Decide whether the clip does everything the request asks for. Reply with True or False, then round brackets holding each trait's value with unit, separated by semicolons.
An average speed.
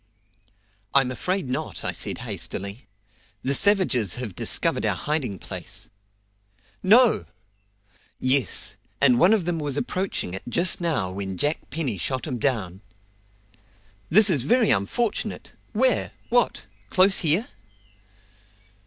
False (120 wpm)